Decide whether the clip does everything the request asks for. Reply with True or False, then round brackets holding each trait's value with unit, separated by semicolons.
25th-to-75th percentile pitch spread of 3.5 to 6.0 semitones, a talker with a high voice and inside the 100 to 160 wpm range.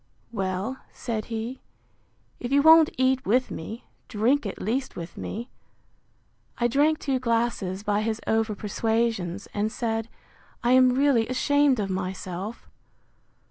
True (3.9 semitones; 230 Hz; 135 wpm)